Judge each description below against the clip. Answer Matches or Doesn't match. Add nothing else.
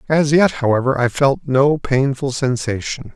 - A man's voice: Matches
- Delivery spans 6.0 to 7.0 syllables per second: Doesn't match